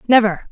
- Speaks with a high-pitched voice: Yes, high, 215 Hz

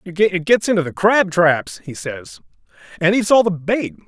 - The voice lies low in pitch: No, medium, 180 Hz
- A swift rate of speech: No, average, 190 wpm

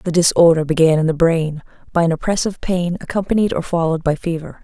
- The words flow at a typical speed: Yes, average, 195 wpm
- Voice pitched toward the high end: No, medium, 170 Hz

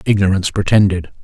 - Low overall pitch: Yes, very low, 95 Hz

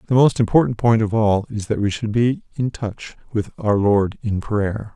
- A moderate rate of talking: No, fast, 220 wpm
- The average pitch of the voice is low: Yes, low, 110 Hz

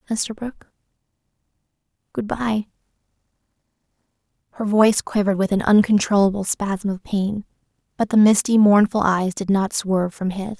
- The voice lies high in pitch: Yes, high, 205 Hz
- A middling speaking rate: No, slow, 125 wpm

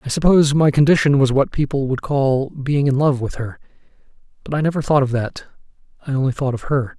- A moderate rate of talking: No, fast, 215 wpm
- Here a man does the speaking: Yes, male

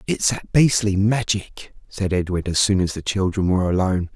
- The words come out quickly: No, average, 190 wpm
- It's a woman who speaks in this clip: No, male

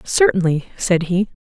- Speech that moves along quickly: No, slow, 125 wpm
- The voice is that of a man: No, female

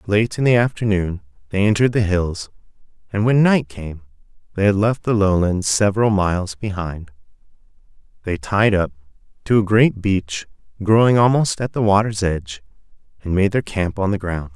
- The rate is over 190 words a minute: No, average, 165 wpm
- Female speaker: No, male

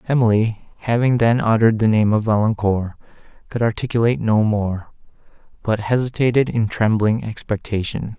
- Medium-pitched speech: No, low, 110 Hz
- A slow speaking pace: Yes, slow, 125 wpm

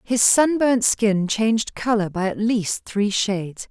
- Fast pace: No, average, 160 wpm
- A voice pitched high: Yes, high, 215 Hz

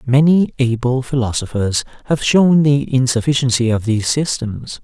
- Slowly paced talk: Yes, slow, 125 wpm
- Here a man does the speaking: Yes, male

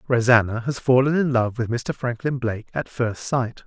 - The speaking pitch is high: No, low, 120 Hz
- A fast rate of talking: No, average, 195 wpm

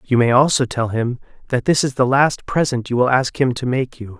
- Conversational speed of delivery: No, fast, 255 wpm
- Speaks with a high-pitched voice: No, low, 125 Hz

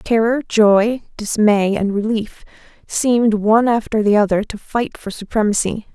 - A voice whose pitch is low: No, high, 215 Hz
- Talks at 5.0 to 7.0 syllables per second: No, 4.6 syllables/s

